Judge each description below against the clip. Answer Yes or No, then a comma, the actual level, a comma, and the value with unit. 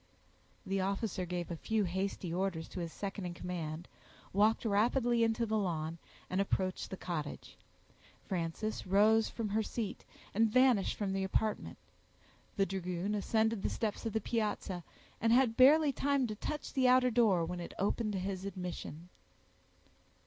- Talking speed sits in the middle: Yes, average, 160 wpm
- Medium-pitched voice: No, high, 200 Hz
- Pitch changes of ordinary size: Yes, average, 3.7 semitones